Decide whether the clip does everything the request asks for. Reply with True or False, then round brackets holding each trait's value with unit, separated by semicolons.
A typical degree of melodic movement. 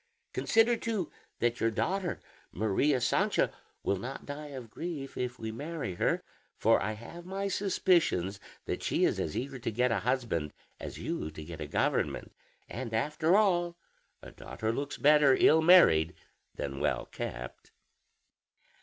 False (7.6 semitones)